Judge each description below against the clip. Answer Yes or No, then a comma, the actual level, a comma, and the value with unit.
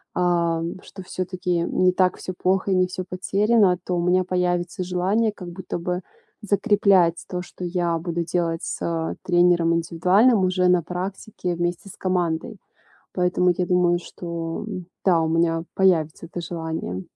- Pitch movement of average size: No, narrow, 1.5 semitones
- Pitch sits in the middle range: Yes, medium, 180 Hz